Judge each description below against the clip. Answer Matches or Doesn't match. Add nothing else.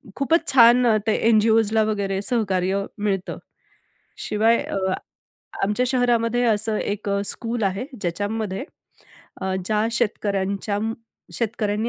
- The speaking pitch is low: Doesn't match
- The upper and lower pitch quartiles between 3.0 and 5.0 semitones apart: Doesn't match